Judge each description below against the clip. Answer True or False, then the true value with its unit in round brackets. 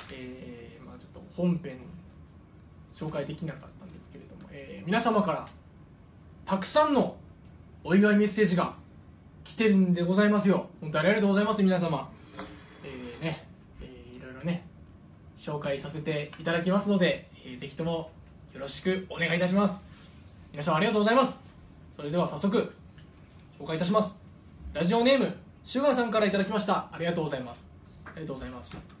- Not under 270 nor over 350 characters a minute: False (365 characters per minute)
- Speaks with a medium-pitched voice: True (170 Hz)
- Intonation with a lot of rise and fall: True (6.4 semitones)